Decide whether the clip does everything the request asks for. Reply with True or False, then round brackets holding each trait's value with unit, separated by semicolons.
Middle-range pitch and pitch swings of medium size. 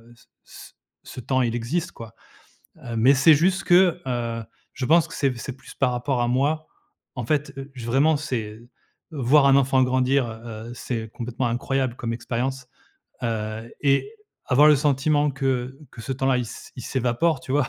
False (130 Hz; 3.0 semitones)